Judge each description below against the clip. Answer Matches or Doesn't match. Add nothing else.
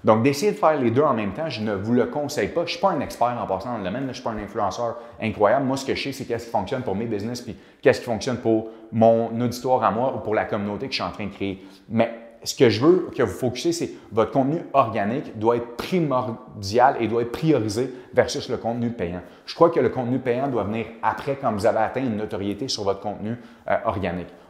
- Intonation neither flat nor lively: Matches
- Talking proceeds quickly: Matches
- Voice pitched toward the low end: Matches